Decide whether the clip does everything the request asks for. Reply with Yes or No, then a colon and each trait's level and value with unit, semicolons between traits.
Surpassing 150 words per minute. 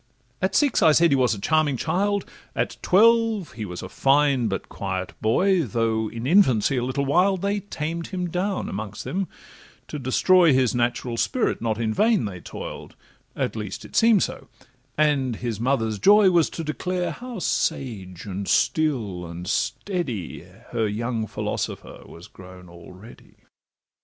Yes: average, 160 wpm